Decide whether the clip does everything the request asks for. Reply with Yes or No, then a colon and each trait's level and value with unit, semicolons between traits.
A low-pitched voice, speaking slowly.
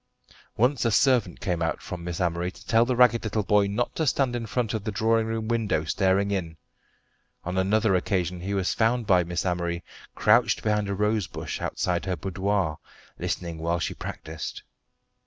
No: low, 100 Hz; average, 185 wpm